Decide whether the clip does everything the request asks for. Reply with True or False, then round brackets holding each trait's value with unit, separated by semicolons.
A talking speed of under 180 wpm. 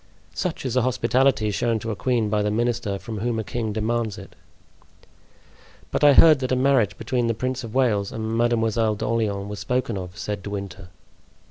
False (195 wpm)